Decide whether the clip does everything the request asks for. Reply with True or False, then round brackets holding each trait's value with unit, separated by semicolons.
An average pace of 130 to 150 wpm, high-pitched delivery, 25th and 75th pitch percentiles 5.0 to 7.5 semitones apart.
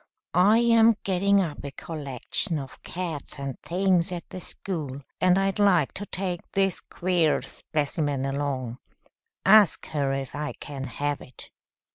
False (145 wpm; 165 Hz; 5.4 semitones)